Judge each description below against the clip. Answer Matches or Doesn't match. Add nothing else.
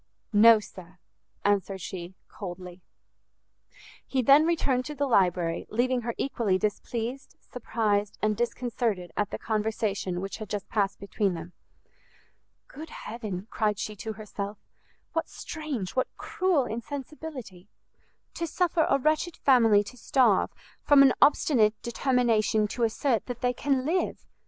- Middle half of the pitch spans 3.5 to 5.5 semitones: Matches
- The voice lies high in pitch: Matches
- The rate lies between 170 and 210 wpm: Doesn't match